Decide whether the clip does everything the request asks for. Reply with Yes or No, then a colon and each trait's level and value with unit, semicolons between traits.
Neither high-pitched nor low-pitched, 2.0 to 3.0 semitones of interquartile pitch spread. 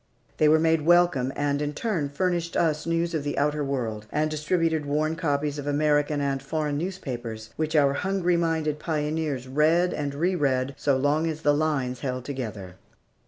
Yes: medium, 150 Hz; narrow, 2.5 semitones